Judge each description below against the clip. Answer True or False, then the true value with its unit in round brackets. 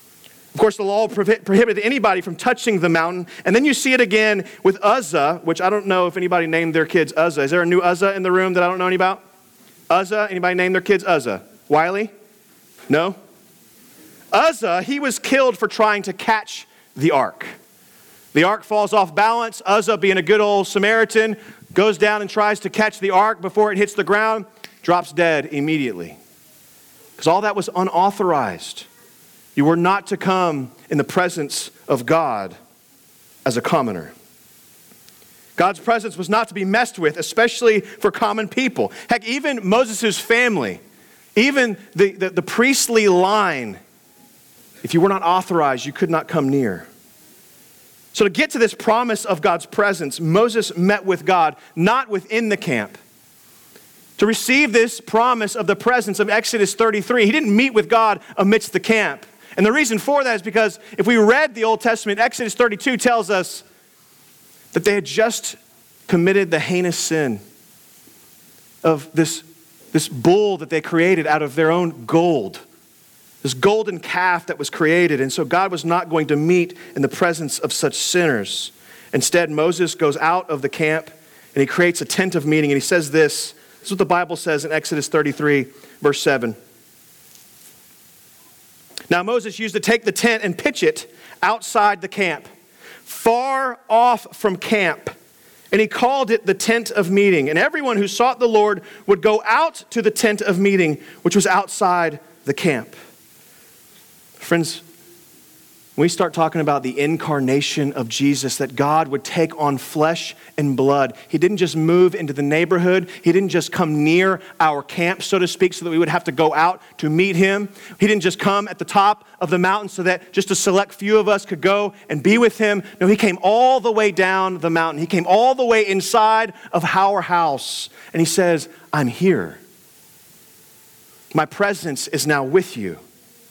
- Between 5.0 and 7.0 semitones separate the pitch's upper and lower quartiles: False (4.4 semitones)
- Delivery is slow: False (180 wpm)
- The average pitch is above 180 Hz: True (190 Hz)